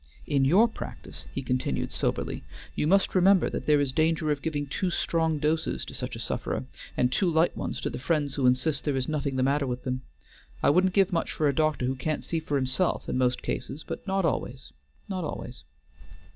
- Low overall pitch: No, medium, 150 Hz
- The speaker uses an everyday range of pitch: Yes, average, 3.9 semitones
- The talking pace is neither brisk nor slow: No, fast, 215 wpm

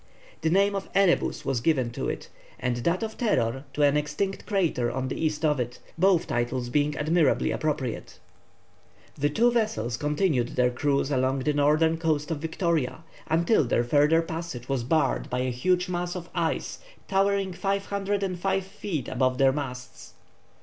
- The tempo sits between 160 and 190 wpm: Yes, average, 165 wpm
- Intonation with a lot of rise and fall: Yes, wide, 5.7 semitones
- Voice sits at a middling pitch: Yes, medium, 150 Hz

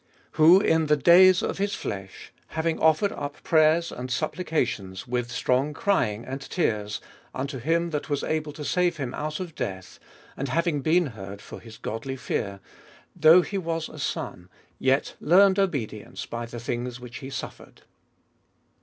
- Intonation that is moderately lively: No, wide, 5.7 semitones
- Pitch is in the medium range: Yes, medium, 145 Hz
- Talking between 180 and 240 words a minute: No, average, 170 wpm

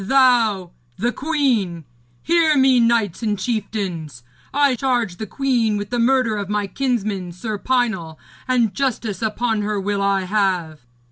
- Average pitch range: Yes, average, 4.3 semitones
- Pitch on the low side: No, high, 220 Hz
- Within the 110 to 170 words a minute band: Yes, average, 145 wpm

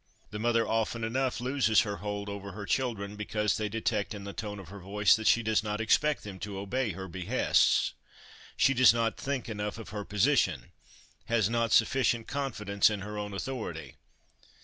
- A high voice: No, low, 105 Hz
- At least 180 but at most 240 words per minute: Yes, average, 185 wpm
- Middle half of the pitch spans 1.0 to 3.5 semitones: Yes, narrow, 2.5 semitones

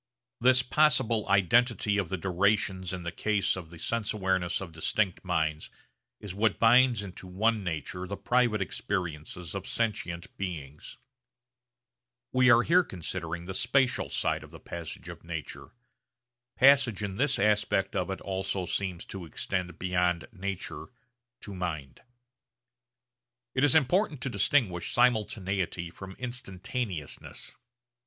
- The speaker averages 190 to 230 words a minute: No, slow, 135 wpm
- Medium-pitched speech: No, very low, 95 Hz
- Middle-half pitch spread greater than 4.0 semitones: Yes, average, 4.7 semitones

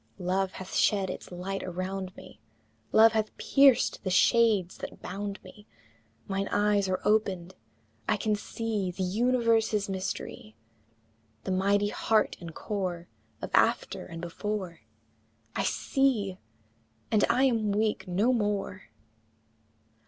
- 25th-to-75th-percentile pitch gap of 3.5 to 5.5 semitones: No, average, 2.8 semitones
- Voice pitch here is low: No, high, 200 Hz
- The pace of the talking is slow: Yes, slow, 125 wpm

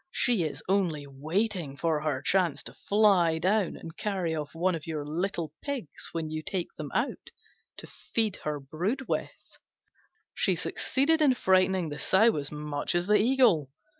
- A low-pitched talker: No, medium, 175 Hz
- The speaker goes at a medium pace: Yes, average, 165 wpm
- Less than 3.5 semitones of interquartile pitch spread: No, average, 5.2 semitones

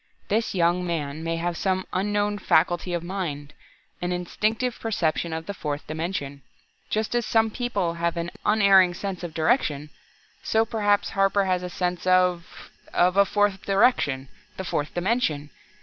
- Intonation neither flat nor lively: Yes, average, 3.6 semitones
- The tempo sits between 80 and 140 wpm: No, average, 155 wpm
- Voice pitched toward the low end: No, medium, 180 Hz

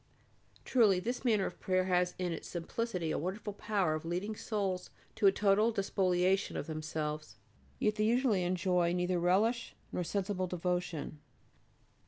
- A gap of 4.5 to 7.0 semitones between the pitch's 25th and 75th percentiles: No, average, 2.9 semitones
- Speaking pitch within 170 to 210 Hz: Yes, medium, 185 Hz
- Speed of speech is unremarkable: Yes, average, 150 wpm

